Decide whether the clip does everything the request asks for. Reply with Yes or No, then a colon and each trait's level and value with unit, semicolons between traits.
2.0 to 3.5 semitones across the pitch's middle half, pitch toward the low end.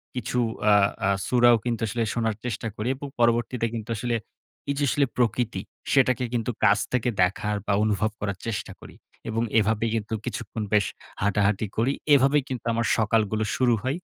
Yes: average, 2.7 semitones; low, 115 Hz